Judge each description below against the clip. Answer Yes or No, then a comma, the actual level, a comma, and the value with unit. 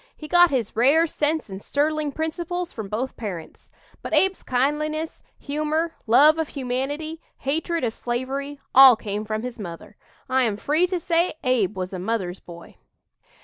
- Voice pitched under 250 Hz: No, very high, 275 Hz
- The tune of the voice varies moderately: No, wide, 5.9 semitones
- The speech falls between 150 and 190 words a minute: Yes, average, 160 wpm